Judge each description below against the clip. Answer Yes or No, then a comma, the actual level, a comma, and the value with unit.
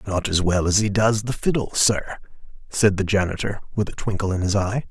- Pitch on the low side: Yes, low, 100 Hz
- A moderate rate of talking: No, fast, 220 wpm